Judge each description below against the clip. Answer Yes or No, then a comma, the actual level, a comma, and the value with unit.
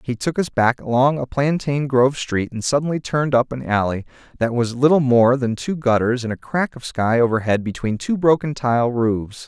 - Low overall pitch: Yes, low, 130 Hz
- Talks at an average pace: No, fast, 210 wpm